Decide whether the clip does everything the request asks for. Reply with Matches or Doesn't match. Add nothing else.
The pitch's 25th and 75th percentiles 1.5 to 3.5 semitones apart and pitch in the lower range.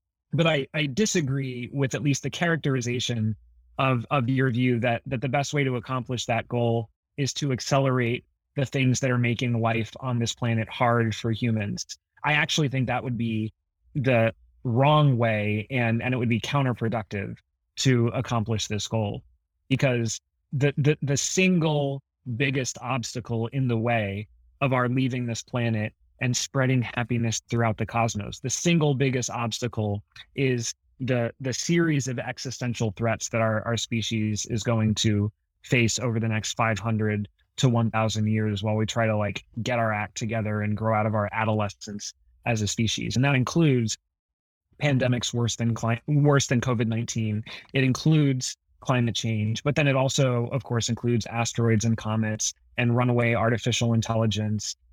Matches